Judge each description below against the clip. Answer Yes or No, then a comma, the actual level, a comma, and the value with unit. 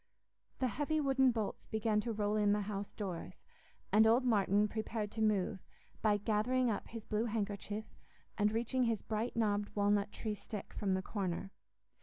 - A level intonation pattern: Yes, narrow, 1.9 semitones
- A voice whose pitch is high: Yes, high, 215 Hz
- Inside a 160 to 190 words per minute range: Yes, average, 170 wpm